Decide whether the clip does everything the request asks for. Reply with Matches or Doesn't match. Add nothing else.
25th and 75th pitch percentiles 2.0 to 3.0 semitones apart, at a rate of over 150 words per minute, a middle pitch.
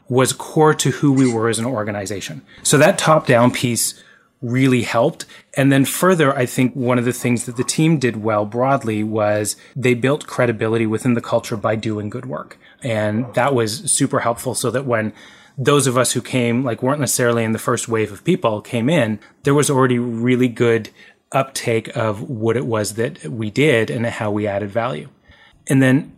Doesn't match